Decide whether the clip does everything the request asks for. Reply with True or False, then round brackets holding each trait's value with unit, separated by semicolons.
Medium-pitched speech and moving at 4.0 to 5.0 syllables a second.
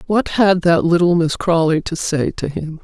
True (170 Hz; 4.6 syllables/s)